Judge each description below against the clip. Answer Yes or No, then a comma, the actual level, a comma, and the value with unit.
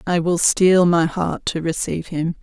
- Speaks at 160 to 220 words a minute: Yes, average, 200 wpm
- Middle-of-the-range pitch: Yes, medium, 170 Hz